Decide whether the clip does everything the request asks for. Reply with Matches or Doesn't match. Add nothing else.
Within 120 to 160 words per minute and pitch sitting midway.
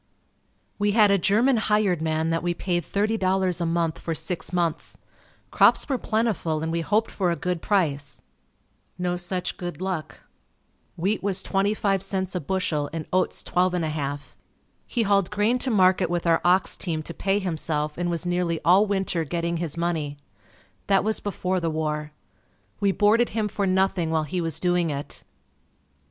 Doesn't match